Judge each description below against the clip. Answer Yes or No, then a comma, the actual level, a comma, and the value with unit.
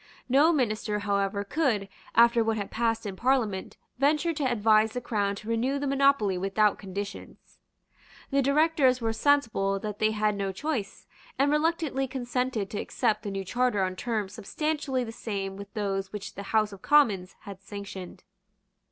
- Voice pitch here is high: Yes, high, 220 Hz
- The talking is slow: No, average, 165 wpm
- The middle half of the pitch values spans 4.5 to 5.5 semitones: Yes, average, 4.9 semitones